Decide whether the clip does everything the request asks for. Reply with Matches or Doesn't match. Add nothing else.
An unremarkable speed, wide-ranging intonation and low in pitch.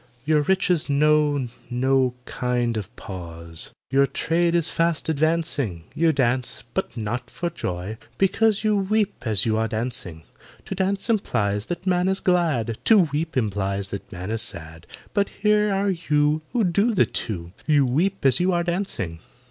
Doesn't match